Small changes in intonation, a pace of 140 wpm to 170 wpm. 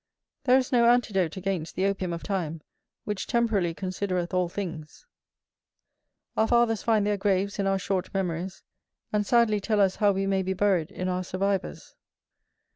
Yes: narrow, 2.2 semitones; average, 165 wpm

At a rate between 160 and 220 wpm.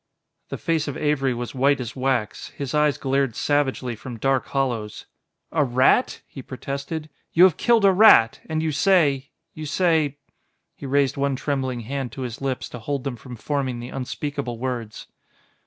Yes: average, 175 wpm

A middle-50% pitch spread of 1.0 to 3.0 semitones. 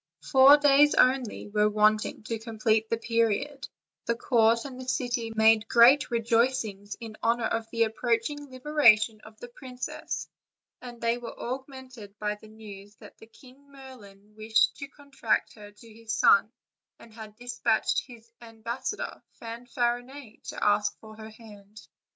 Yes: average, 2.7 semitones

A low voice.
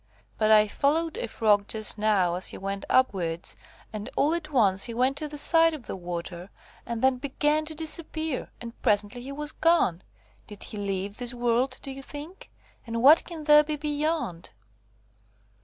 No: very high, 250 Hz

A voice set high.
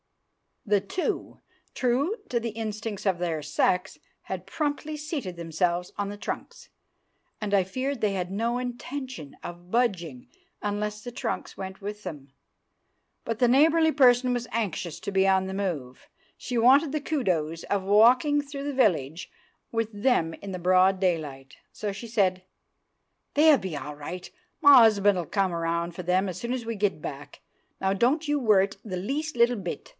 Yes: high, 205 Hz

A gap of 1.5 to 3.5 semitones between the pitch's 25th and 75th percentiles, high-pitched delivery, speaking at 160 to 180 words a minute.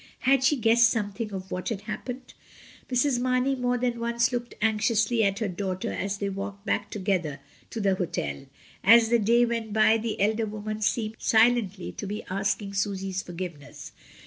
Yes: average, 3.1 semitones; high, 215 Hz; average, 170 wpm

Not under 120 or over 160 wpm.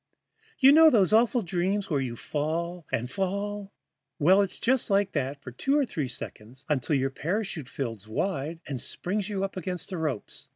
No: average, 180 wpm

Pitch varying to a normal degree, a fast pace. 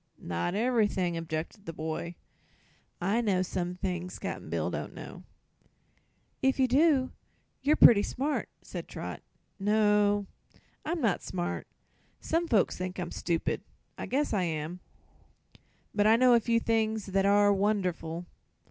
No: average, 4.5 semitones; average, 140 wpm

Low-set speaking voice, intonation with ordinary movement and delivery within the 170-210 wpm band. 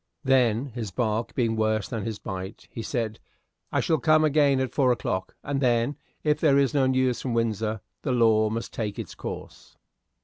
Yes: low, 120 Hz; average, 3.6 semitones; average, 190 wpm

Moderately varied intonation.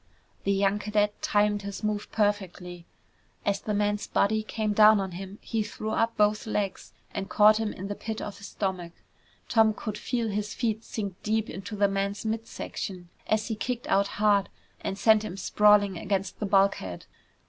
No: narrow, 1.5 semitones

